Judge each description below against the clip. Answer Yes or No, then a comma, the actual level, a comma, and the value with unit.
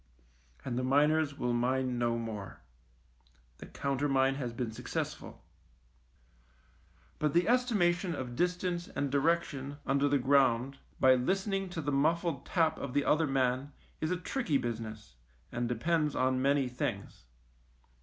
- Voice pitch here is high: No, medium, 140 Hz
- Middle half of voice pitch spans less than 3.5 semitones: No, average, 4.5 semitones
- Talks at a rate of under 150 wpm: Yes, average, 140 wpm